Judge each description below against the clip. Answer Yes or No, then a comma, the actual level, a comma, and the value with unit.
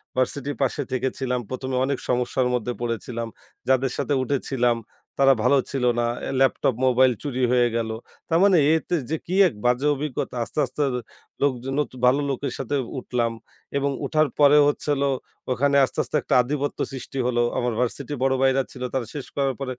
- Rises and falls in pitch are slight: Yes, narrow, 2.3 semitones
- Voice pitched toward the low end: Yes, low, 130 Hz